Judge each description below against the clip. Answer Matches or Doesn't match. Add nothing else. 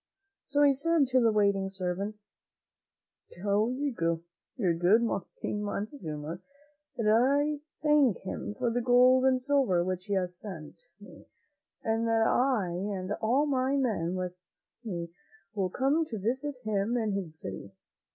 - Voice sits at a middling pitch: Doesn't match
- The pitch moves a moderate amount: Doesn't match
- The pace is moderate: Matches